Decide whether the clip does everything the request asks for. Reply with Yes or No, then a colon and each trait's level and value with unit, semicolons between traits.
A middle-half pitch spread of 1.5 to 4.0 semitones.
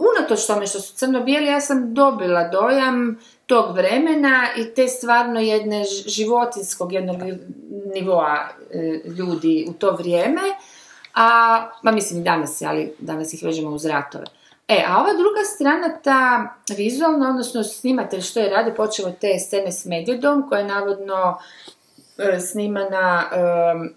No: wide, 5.6 semitones